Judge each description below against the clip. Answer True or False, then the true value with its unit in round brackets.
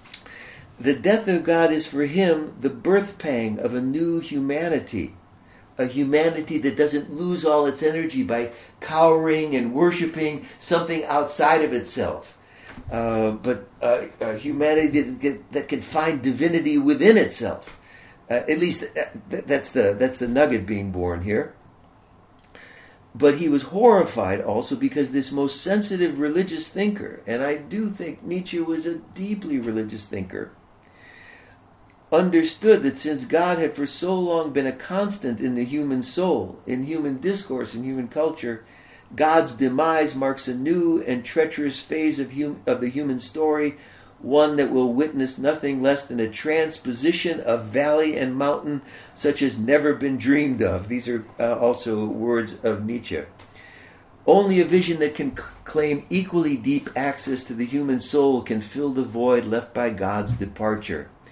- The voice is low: False (145 Hz)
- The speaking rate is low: False (155 wpm)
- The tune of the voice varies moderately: True (4.5 semitones)